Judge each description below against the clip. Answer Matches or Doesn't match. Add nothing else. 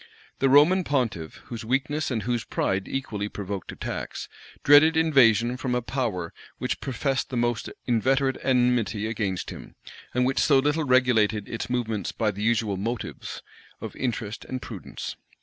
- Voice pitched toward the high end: Doesn't match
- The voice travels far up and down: Doesn't match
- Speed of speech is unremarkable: Matches